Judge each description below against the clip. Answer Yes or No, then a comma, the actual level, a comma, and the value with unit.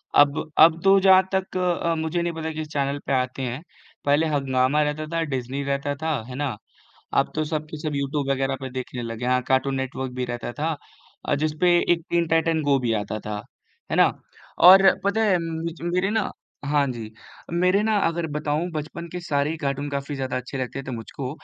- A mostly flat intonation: No, average, 3.8 semitones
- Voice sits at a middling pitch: Yes, medium, 145 Hz